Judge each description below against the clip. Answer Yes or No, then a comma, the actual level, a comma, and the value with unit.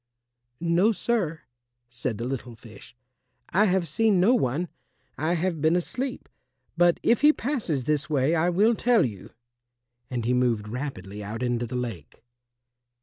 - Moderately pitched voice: Yes, medium, 155 Hz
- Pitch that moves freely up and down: Yes, wide, 7.4 semitones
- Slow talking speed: No, average, 150 wpm